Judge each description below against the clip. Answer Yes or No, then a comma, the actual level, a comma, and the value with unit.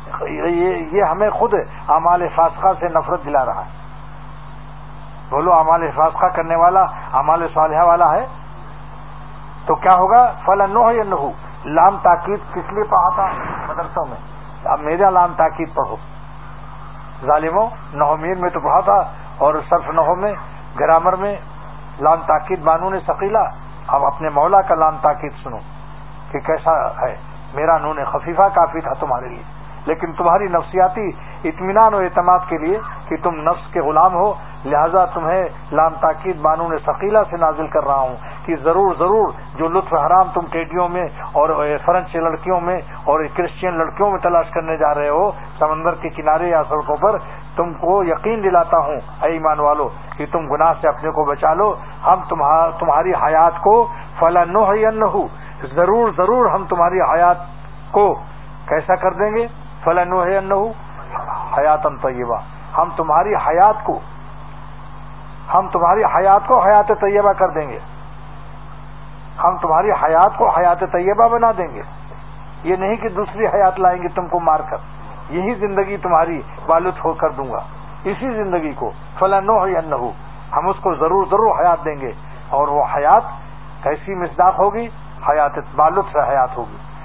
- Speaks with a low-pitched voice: No, medium, 170 Hz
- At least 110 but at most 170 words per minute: Yes, average, 155 wpm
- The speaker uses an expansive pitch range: No, average, 3.4 semitones